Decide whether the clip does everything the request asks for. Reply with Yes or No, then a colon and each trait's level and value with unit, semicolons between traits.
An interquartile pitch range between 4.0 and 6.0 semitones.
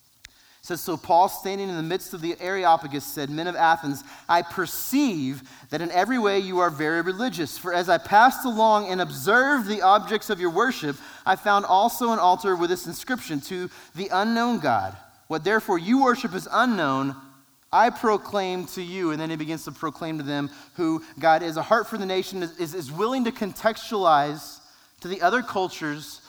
Yes: average, 4.8 semitones